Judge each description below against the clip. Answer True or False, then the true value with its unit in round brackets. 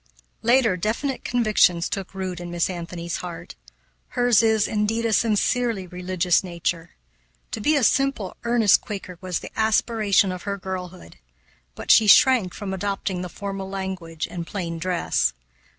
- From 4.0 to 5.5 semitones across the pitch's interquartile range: False (3.6 semitones)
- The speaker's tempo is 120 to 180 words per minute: True (150 wpm)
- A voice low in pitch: False (190 Hz)